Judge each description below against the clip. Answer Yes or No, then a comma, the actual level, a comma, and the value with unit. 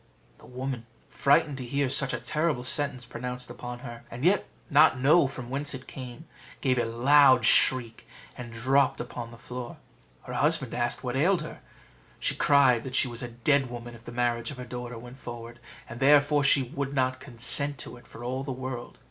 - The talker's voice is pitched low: Yes, low, 125 Hz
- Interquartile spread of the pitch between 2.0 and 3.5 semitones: Yes, average, 2.7 semitones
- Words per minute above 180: Yes, average, 200 wpm